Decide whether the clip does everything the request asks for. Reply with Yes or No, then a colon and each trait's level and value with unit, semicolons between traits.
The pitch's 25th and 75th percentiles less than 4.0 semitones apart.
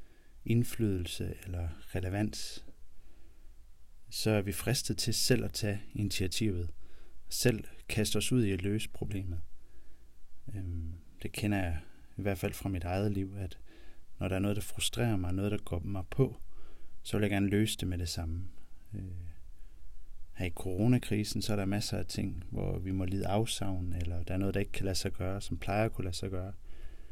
Yes: average, 3.5 semitones